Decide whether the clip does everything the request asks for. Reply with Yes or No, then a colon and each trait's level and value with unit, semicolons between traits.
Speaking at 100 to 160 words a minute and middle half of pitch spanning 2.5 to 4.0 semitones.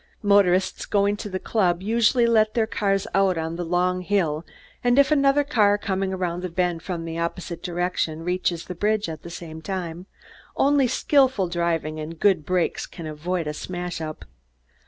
No: average, 175 wpm; average, 3.4 semitones